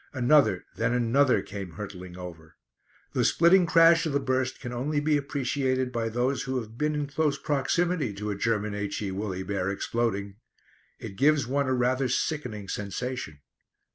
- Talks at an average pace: Yes, average, 165 wpm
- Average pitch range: No, wide, 5.7 semitones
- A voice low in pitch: Yes, low, 125 Hz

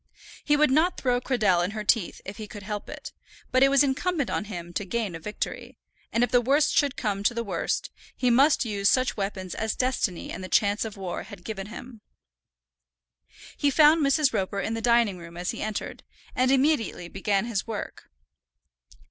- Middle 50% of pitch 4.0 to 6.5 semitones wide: Yes, average, 4.7 semitones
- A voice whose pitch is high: Yes, high, 225 Hz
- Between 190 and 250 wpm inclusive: Yes, average, 200 wpm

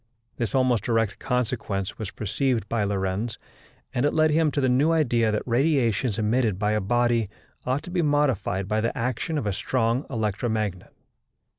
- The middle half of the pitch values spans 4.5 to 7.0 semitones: No, average, 3.7 semitones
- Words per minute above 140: Yes, average, 170 wpm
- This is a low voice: Yes, low, 115 Hz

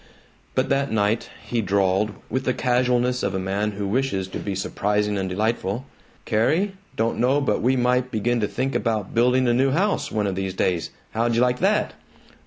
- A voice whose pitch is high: No, low, 115 Hz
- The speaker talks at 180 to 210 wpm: Yes, average, 195 wpm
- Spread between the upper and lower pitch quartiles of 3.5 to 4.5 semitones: Yes, average, 3.9 semitones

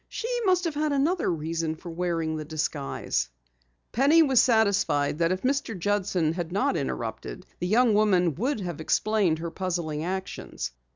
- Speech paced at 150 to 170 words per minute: Yes, average, 160 wpm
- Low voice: No, medium, 185 Hz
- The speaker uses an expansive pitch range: Yes, wide, 7.3 semitones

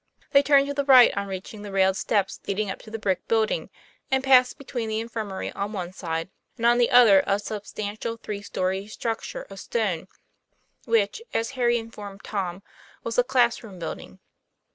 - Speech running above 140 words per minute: Yes, average, 185 wpm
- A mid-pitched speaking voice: No, high, 215 Hz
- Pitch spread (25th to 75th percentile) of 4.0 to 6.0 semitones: No, average, 3.4 semitones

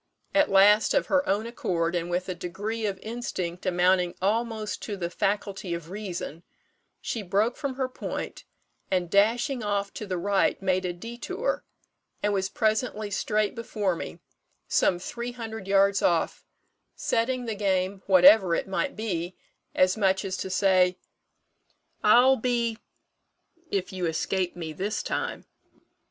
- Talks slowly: No, average, 145 wpm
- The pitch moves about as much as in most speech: Yes, average, 3.4 semitones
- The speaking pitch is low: No, high, 200 Hz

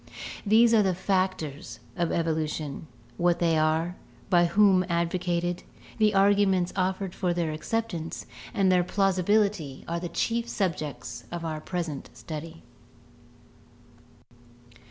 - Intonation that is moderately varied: Yes, average, 3.0 semitones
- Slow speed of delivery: Yes, slow, 115 wpm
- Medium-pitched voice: Yes, medium, 175 Hz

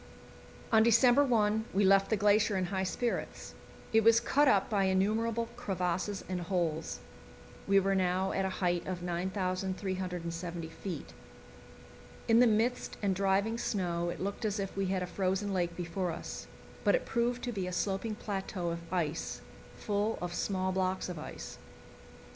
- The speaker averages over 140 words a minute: Yes, average, 165 wpm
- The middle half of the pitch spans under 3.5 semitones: Yes, average, 2.9 semitones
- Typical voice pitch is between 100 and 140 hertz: No, high, 190 Hz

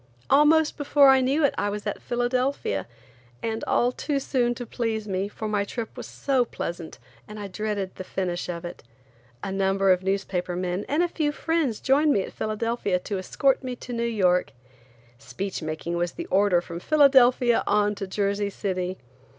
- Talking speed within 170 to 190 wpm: Yes, average, 180 wpm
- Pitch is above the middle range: Yes, high, 210 Hz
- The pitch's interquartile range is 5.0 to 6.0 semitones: Yes, average, 5.3 semitones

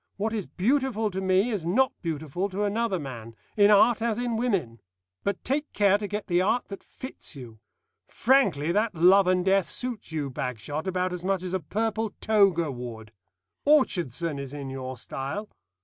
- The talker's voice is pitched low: No, high, 190 Hz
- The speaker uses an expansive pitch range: Yes, wide, 6.3 semitones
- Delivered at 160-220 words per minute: Yes, average, 180 wpm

